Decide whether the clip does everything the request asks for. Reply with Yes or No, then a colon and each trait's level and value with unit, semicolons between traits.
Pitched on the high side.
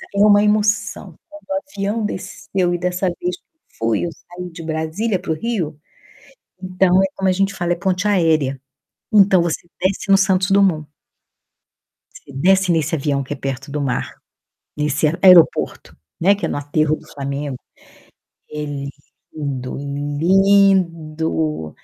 No: medium, 175 Hz